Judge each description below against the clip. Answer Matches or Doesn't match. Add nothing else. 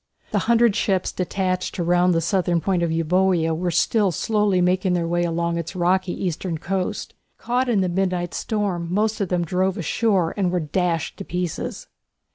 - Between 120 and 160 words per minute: Doesn't match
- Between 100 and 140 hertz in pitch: Doesn't match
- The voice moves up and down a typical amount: Doesn't match